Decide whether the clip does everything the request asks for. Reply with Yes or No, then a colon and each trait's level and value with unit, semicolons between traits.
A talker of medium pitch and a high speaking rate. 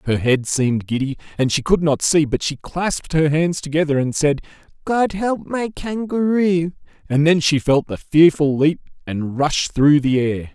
No: medium, 155 Hz; average, 190 wpm